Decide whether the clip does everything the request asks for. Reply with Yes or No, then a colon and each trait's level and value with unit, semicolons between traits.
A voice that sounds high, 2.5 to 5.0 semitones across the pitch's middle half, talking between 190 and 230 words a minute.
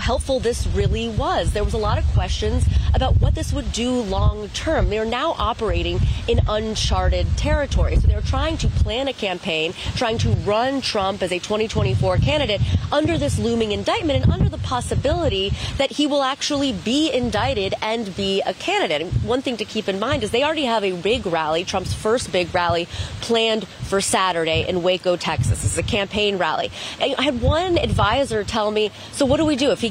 No: high, 210 Hz; wide, 5.5 semitones; average, 195 wpm